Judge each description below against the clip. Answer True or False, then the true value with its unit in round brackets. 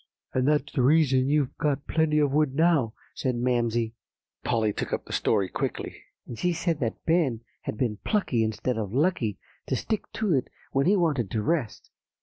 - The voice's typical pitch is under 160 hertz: True (135 Hz)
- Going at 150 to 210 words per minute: True (185 wpm)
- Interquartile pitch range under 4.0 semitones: False (5.2 semitones)